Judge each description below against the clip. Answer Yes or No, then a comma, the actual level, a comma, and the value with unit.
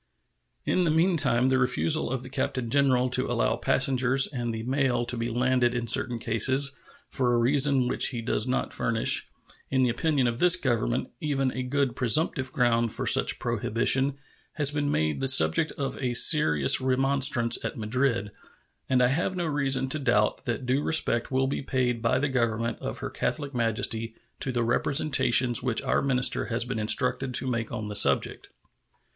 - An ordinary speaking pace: Yes, average, 175 wpm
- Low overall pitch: Yes, low, 125 Hz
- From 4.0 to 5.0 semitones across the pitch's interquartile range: No, narrow, 2.6 semitones